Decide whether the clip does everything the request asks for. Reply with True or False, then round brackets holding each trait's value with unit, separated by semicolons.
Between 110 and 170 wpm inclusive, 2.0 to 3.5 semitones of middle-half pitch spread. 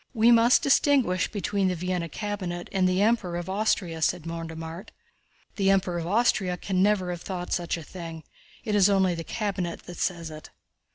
False (185 wpm; 3.0 semitones)